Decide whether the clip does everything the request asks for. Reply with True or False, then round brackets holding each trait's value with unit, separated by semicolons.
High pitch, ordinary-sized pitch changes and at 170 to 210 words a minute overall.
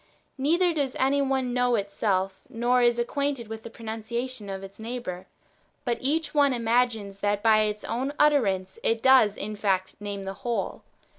True (230 Hz; 4.1 semitones; 175 wpm)